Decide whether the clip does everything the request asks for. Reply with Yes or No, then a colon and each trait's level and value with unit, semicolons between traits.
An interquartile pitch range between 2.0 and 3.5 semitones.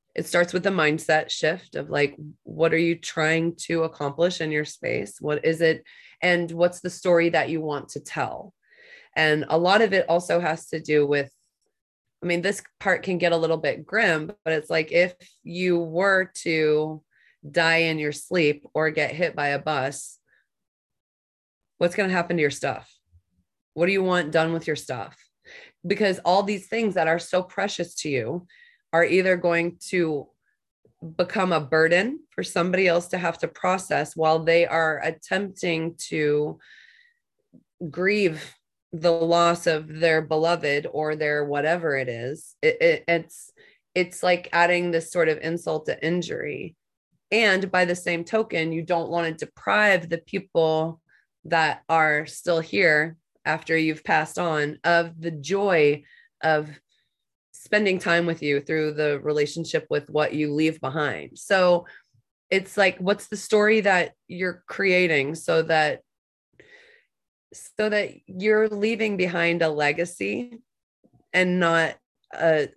Yes: average, 2.9 semitones